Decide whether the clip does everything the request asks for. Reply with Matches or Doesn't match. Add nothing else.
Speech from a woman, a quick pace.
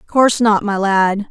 Doesn't match